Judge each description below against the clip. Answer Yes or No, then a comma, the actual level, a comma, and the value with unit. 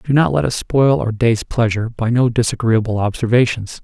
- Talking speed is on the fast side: No, average, 190 wpm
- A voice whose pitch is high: No, low, 115 Hz